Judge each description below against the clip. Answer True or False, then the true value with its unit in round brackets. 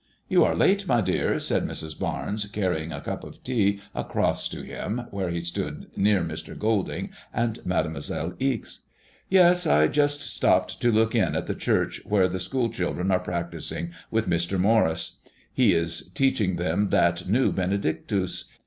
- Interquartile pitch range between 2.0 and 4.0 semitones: False (4.8 semitones)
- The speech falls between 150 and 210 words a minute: True (170 wpm)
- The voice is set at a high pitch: False (100 Hz)